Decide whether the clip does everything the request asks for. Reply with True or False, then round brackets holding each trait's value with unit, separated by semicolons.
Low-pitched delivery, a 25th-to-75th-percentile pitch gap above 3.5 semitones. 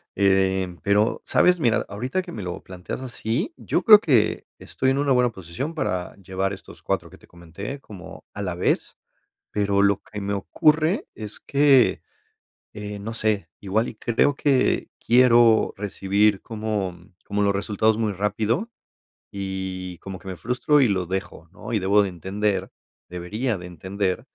True (105 Hz; 3.9 semitones)